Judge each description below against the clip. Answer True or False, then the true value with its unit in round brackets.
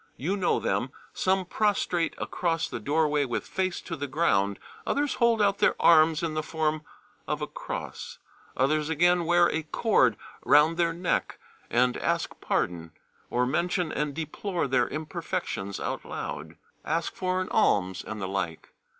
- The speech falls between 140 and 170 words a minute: True (160 wpm)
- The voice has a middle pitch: True (160 Hz)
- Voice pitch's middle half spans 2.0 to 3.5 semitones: False (5.0 semitones)